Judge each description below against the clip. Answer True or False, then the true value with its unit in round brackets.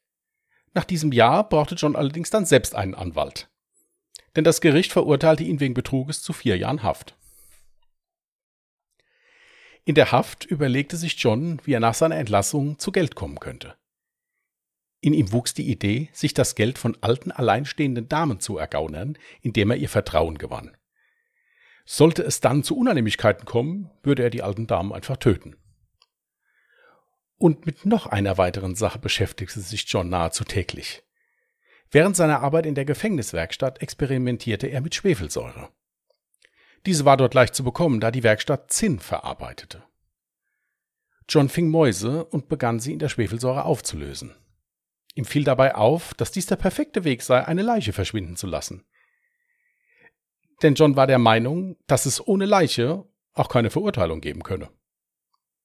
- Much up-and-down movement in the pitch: True (7.1 semitones)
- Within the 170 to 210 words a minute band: False (150 wpm)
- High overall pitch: False (145 Hz)